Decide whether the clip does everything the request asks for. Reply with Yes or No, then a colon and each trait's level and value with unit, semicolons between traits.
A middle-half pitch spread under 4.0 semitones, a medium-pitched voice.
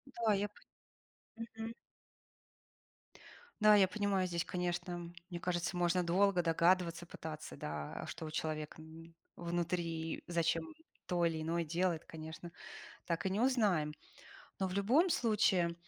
Yes: average, 2.7 semitones; medium, 175 Hz